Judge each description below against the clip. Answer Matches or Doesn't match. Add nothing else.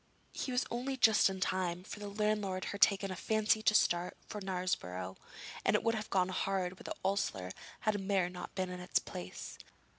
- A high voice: Matches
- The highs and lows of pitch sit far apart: Doesn't match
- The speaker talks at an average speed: Doesn't match